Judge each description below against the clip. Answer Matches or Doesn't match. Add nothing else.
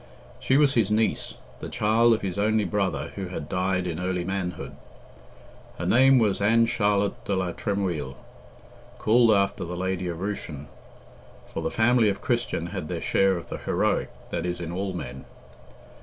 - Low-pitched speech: Matches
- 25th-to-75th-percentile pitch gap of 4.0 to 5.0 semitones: Doesn't match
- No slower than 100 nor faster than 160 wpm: Doesn't match